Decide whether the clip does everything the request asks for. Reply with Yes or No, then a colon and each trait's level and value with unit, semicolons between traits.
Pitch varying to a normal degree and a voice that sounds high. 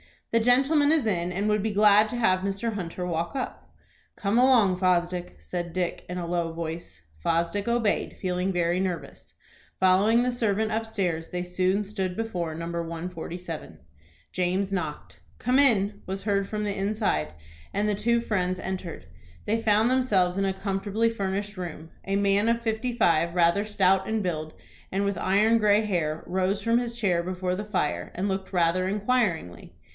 Yes: average, 3.3 semitones; high, 195 Hz